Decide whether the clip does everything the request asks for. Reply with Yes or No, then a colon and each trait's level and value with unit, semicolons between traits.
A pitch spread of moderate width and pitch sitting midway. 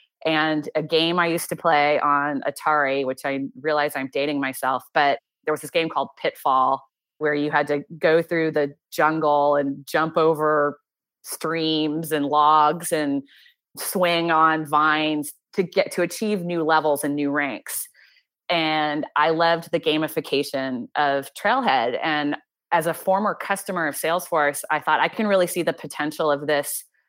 No: narrow, 2.3 semitones; medium, 155 Hz